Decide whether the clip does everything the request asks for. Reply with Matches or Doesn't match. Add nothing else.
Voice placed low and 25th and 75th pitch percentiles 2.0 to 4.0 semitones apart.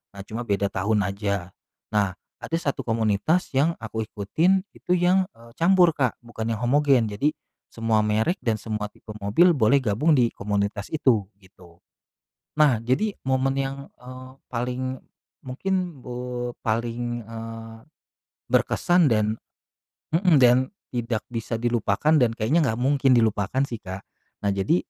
Doesn't match